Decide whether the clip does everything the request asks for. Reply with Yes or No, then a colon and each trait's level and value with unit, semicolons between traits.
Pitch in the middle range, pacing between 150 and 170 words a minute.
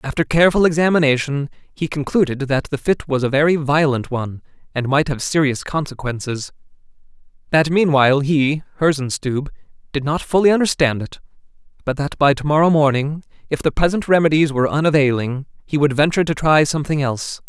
Yes: medium, 145 Hz; average, 160 wpm